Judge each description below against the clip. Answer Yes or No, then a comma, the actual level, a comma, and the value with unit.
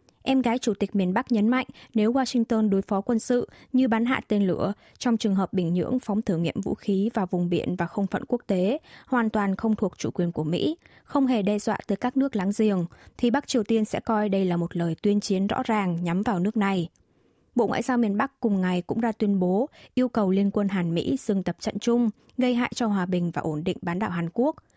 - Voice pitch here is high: Yes, high, 210 Hz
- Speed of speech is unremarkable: No, fast, 255 wpm